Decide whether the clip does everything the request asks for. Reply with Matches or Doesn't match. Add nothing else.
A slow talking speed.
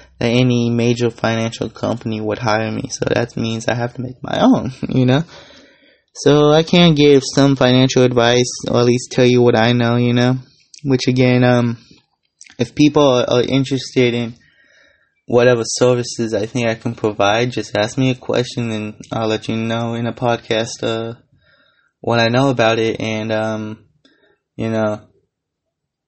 Doesn't match